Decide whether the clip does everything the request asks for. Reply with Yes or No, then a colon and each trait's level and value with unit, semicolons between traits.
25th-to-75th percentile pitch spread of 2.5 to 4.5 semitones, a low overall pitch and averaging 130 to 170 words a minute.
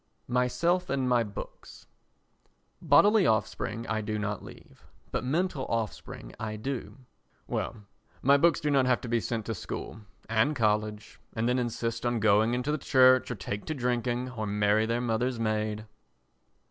Yes: average, 3.0 semitones; low, 115 Hz; average, 160 wpm